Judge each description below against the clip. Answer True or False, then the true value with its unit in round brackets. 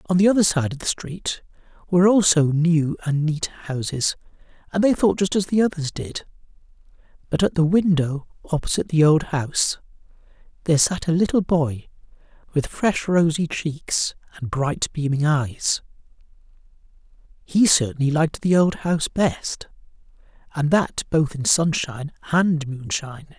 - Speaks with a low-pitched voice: False (160 Hz)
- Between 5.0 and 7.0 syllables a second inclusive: False (4.7 syllables/s)